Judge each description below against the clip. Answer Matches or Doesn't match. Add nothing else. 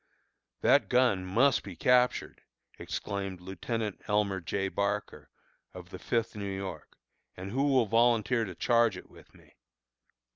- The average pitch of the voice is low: Matches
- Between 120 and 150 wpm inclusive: Matches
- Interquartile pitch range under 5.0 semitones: Matches